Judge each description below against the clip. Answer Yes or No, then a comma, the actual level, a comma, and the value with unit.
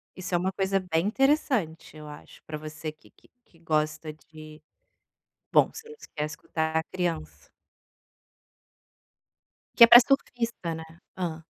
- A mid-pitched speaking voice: Yes, medium, 165 Hz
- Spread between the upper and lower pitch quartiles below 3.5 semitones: No, average, 3.8 semitones